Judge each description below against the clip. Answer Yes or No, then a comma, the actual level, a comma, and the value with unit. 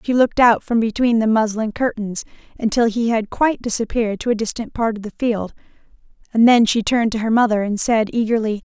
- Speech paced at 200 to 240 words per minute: Yes, fast, 205 wpm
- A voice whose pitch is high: Yes, high, 225 Hz